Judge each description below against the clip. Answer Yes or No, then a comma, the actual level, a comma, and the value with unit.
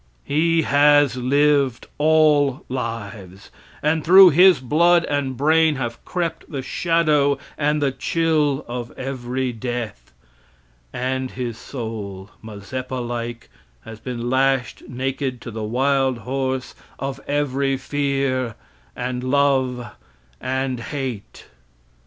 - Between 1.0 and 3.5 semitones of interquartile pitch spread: Yes, average, 3.0 semitones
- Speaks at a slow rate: Yes, slow, 110 wpm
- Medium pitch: No, low, 130 Hz